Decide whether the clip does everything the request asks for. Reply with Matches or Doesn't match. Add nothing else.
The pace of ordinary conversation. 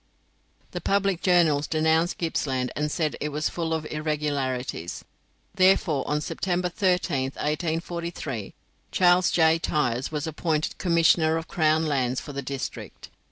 Doesn't match